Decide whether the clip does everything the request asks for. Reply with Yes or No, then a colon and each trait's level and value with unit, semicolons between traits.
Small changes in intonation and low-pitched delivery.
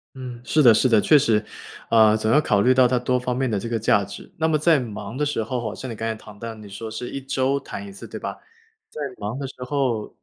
No: average, 3.4 semitones; low, 120 Hz